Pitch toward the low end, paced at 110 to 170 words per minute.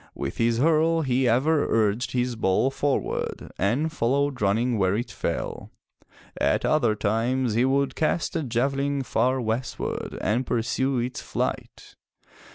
Yes: low, 125 Hz; average, 140 wpm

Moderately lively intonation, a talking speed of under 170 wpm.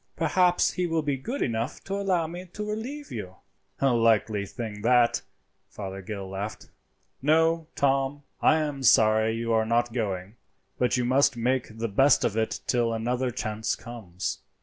Yes: average, 5.0 semitones; average, 160 wpm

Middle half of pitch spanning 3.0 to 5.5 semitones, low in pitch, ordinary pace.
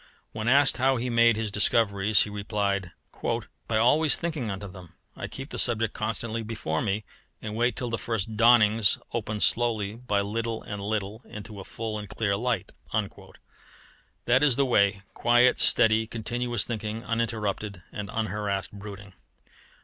No: narrow, 2.5 semitones; low, 110 Hz; average, 155 wpm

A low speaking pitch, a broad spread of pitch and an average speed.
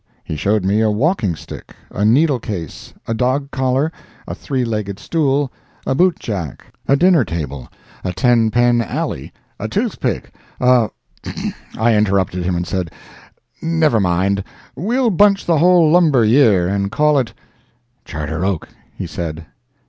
Yes: low, 115 Hz; wide, 7.1 semitones; average, 145 wpm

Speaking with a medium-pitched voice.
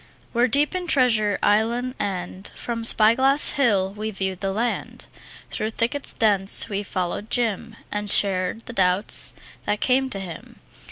No: high, 215 Hz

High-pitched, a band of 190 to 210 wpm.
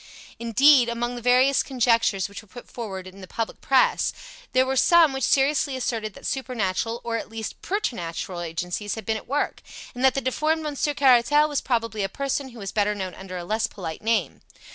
Yes: high, 235 Hz; average, 200 wpm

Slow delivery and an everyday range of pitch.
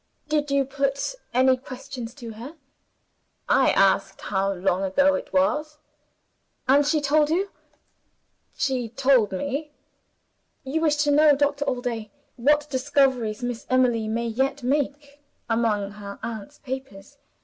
Yes: slow, 130 wpm; average, 3.8 semitones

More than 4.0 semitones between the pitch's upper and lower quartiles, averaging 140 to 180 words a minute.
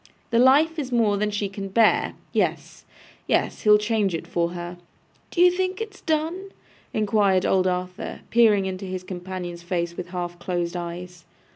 Yes: average, 4.7 semitones; average, 160 wpm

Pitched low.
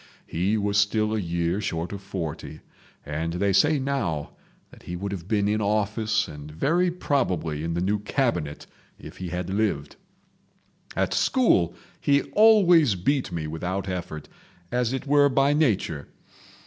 Yes: low, 100 Hz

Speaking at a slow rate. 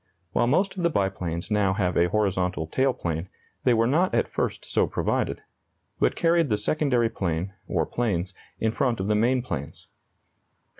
No: average, 170 wpm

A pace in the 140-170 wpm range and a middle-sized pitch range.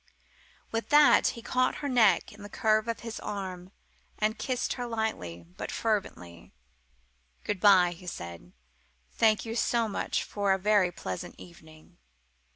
Yes: average, 150 wpm; average, 4.5 semitones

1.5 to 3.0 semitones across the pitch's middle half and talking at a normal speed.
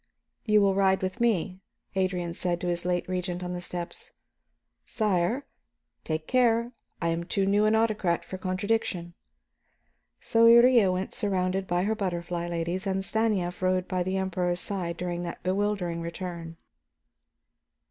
Yes: average, 2.7 semitones; average, 150 wpm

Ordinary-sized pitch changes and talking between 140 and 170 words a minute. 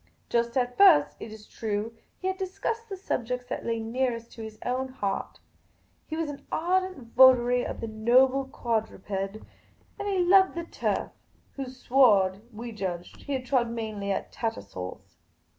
Yes: average, 4.2 semitones; average, 165 wpm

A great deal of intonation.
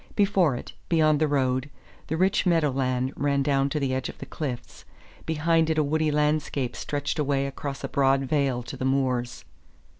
No: average, 2.7 semitones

